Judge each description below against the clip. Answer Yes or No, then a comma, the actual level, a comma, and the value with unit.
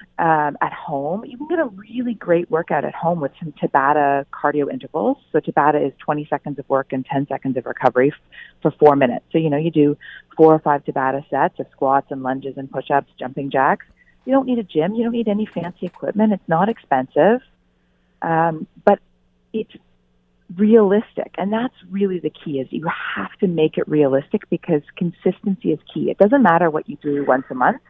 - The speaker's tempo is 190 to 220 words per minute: Yes, average, 200 wpm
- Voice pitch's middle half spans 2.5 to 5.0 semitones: No, wide, 5.4 semitones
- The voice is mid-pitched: Yes, medium, 155 Hz